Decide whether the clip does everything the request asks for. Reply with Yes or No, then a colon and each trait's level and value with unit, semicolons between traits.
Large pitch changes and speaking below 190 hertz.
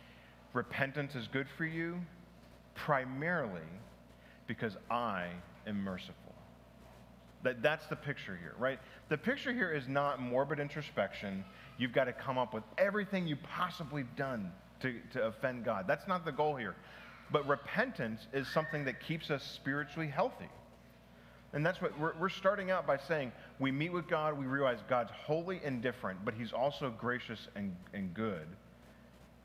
Yes: wide, 6.4 semitones; low, 135 Hz